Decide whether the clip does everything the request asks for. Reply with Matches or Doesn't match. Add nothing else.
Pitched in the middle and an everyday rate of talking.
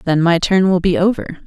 Doesn't match